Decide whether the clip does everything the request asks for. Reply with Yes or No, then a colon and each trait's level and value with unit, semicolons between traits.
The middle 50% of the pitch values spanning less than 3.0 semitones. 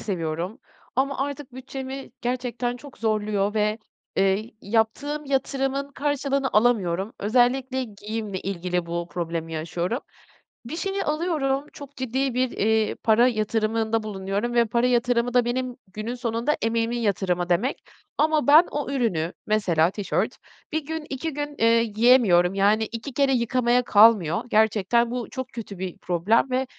No: average, 4.3 semitones